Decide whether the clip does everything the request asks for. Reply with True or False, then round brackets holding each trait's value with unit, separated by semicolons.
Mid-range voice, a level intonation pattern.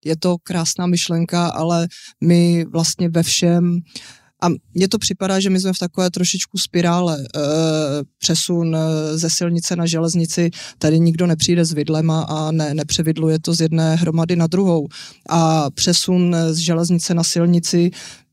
True (170 Hz; 1.5 semitones)